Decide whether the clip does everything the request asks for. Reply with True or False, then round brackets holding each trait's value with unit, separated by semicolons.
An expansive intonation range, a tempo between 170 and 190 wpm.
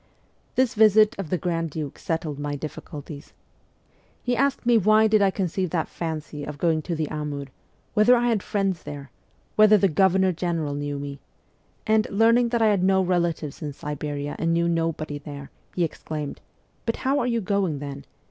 True (6.1 semitones; 185 wpm)